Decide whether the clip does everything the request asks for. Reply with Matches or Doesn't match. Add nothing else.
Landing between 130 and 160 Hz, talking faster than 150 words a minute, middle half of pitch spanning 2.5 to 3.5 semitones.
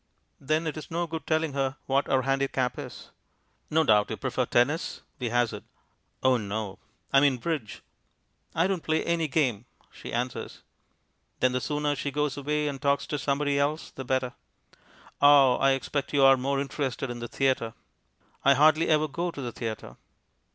Matches